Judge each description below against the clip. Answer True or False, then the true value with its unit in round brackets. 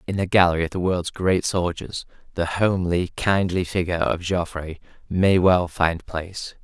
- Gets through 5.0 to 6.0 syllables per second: False (4.8 syllables/s)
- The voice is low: True (90 Hz)